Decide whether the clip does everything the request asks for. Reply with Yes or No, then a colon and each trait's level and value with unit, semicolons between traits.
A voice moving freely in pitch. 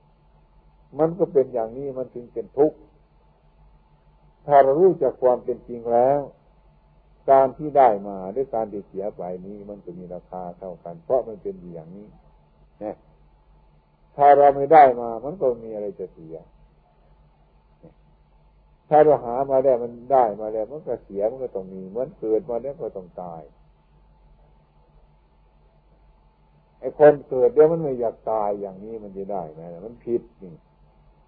Yes: wide, 7.6 semitones